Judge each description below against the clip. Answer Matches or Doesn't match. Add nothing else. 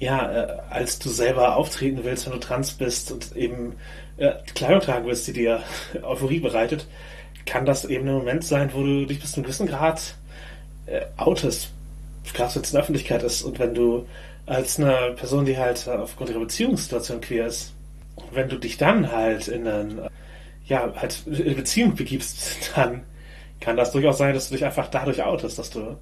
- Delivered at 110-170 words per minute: Doesn't match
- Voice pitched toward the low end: Matches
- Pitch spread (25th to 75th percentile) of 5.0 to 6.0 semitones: Doesn't match